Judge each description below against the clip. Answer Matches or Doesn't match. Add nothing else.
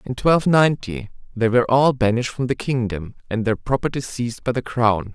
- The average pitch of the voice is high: Doesn't match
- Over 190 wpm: Matches